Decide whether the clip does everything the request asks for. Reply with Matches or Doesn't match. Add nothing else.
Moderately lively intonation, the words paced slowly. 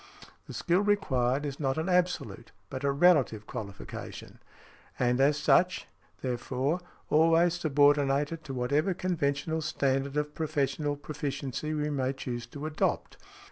Matches